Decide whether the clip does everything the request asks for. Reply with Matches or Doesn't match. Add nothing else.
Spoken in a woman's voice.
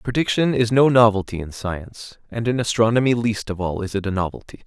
Doesn't match